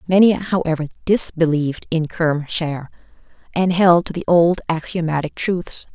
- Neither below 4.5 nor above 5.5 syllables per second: Yes, 4.6 syllables/s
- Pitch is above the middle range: No, medium, 170 Hz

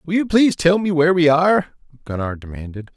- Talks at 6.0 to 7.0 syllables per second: Yes, 6.1 syllables/s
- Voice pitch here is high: No, medium, 150 Hz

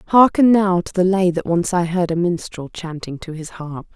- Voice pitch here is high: No, medium, 175 Hz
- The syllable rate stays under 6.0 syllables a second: Yes, 5.0 syllables/s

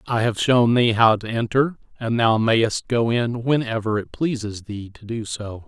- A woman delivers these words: No, male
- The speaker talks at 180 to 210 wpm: Yes, average, 200 wpm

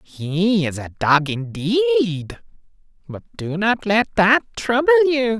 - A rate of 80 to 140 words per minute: Yes, slow, 135 wpm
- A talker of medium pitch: No, high, 210 Hz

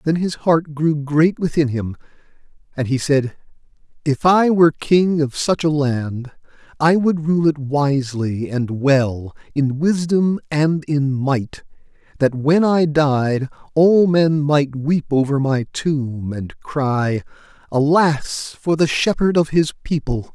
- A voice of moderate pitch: Yes, medium, 145 Hz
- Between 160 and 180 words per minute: No, average, 145 wpm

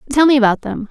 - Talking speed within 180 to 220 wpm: No, fast, 265 wpm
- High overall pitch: Yes, very high, 255 Hz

